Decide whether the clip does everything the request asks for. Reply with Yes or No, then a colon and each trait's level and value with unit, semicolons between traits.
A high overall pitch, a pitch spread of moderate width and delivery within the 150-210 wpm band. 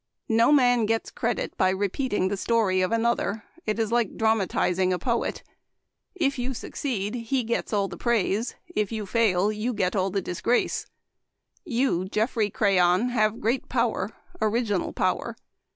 Yes: high, 220 Hz; average, 3.5 semitones; average, 160 wpm